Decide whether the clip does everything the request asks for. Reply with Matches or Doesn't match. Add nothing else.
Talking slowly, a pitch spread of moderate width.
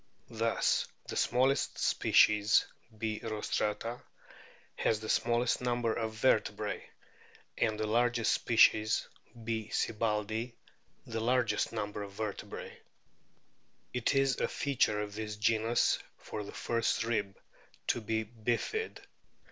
Doesn't match